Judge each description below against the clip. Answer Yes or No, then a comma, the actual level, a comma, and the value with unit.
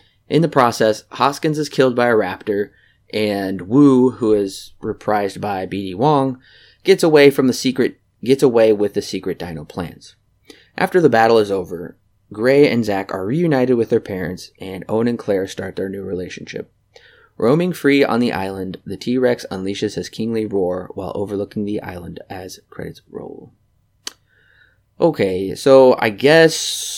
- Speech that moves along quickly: No, average, 160 wpm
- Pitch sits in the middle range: No, low, 110 Hz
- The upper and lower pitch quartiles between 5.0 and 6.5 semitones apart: Yes, wide, 5.4 semitones